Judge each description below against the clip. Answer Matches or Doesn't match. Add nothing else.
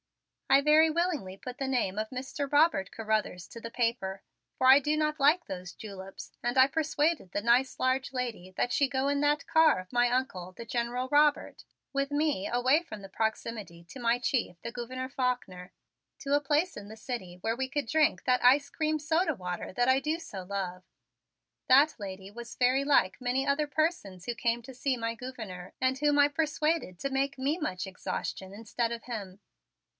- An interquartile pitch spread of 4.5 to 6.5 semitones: Matches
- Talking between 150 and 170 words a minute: Doesn't match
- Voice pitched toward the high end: Matches